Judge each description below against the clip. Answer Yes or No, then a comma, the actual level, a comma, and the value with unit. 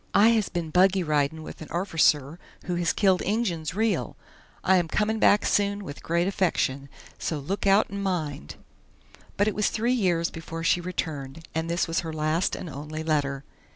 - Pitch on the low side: No, medium, 170 Hz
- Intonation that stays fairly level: No, average, 4.1 semitones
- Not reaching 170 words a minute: No, average, 185 wpm